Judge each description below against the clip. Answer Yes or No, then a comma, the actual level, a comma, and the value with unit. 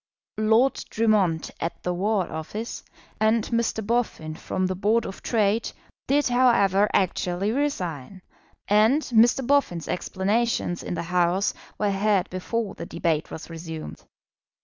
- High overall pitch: Yes, high, 200 Hz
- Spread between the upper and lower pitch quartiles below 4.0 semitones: No, average, 4.4 semitones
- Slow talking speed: Yes, slow, 130 wpm